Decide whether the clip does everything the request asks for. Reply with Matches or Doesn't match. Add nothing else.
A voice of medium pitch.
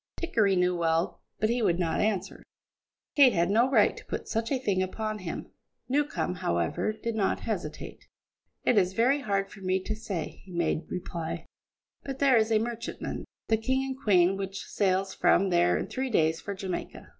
Doesn't match